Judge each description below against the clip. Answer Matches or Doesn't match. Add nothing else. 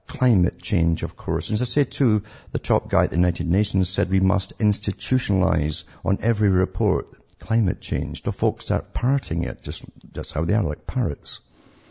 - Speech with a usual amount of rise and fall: Matches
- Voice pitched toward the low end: Matches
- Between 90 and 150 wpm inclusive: Doesn't match